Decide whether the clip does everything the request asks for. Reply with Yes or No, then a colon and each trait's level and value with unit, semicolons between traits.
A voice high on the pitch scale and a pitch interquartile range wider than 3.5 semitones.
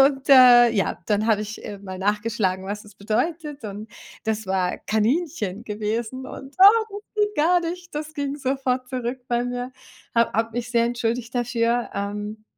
Yes: high, 235 Hz; average, 4.1 semitones